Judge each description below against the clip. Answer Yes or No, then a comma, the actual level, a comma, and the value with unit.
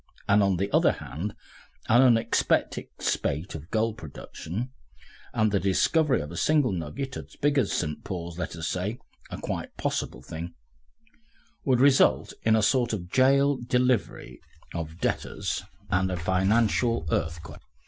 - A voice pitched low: Yes, low, 100 Hz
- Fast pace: No, average, 145 wpm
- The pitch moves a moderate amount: No, wide, 6.5 semitones